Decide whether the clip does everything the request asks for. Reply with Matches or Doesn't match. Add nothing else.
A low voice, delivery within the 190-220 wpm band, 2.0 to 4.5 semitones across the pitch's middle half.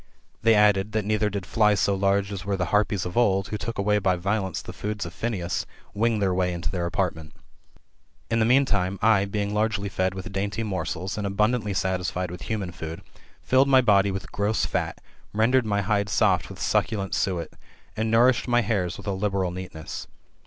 Matches